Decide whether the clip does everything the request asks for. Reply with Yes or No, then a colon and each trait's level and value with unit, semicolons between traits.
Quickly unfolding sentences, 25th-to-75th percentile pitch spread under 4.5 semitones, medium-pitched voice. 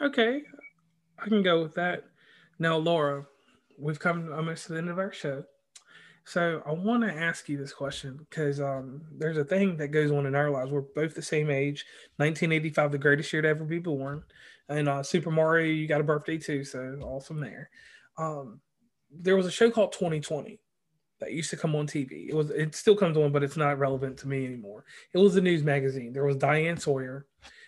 Yes: fast, 210 wpm; average, 3.1 semitones; medium, 155 Hz